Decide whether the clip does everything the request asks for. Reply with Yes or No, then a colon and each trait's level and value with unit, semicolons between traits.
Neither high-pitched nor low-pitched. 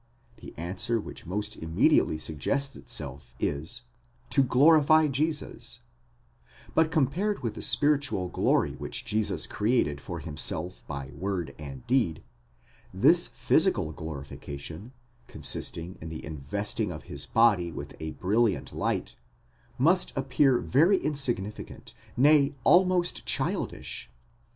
No: low, 105 Hz